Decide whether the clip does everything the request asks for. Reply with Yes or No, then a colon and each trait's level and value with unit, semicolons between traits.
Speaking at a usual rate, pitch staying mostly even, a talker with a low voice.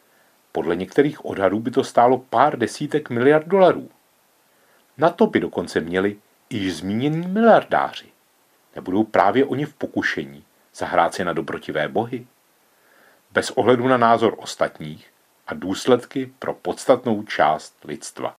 No: average, 130 wpm; wide, 5.5 semitones; low, 130 Hz